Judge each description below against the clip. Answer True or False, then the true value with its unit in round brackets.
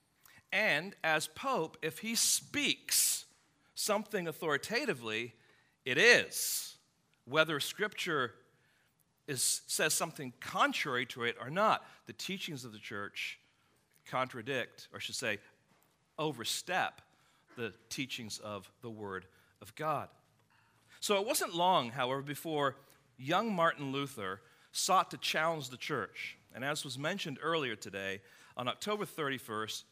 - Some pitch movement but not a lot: False (5.9 semitones)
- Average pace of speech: False (120 wpm)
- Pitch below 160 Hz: True (140 Hz)